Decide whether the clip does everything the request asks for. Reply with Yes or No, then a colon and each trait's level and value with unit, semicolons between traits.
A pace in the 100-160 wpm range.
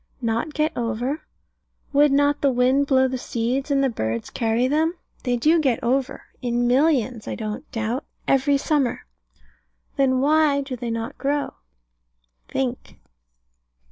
Yes: average, 140 wpm